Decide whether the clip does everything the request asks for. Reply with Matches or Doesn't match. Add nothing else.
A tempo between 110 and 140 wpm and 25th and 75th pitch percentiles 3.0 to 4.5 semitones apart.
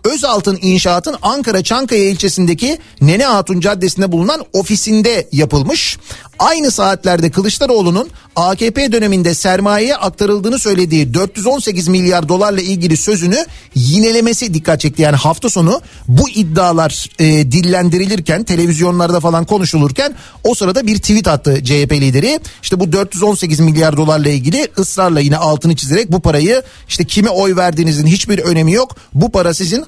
Matches